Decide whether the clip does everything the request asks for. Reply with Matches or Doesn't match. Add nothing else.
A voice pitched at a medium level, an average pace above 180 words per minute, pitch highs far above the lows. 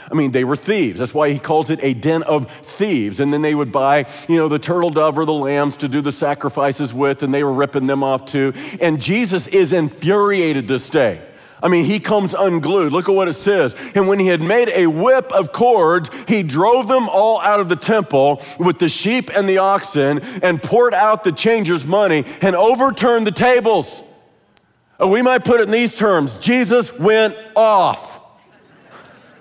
Matches